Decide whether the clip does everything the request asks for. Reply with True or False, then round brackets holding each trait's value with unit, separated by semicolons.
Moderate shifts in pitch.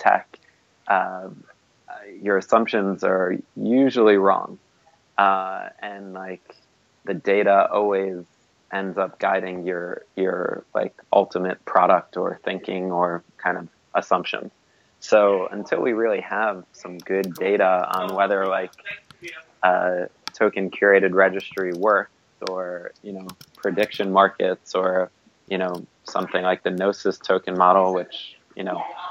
False (1.4 semitones)